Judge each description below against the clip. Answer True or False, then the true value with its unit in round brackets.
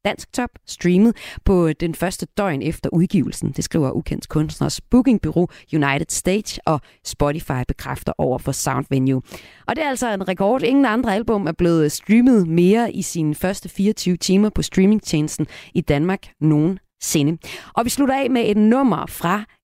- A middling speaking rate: True (160 wpm)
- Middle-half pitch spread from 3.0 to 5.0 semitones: False (5.5 semitones)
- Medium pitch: True (180 Hz)